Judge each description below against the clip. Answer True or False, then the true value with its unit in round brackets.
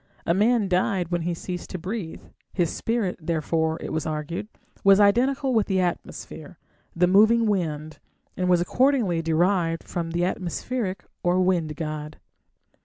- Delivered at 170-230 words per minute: False (150 wpm)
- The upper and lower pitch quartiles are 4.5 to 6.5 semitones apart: False (3.5 semitones)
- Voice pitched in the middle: True (180 Hz)